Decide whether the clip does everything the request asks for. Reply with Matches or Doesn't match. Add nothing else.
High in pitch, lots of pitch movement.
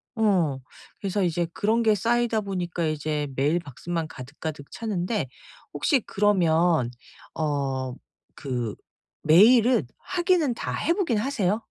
Doesn't match